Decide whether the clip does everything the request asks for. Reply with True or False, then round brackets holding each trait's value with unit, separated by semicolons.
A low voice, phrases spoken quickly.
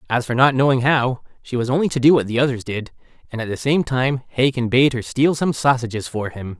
True (130 Hz; 245 wpm)